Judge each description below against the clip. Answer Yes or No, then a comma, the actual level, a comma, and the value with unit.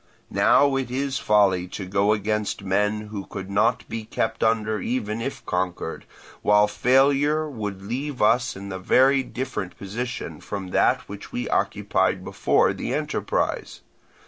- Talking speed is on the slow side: No, average, 145 wpm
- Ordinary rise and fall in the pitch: Yes, average, 4.2 semitones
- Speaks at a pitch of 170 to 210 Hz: No, low, 105 Hz